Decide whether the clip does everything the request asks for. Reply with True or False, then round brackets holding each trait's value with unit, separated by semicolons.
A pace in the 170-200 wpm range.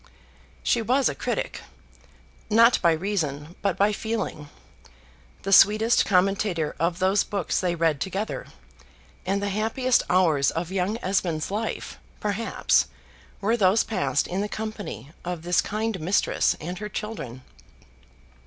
False (135 wpm)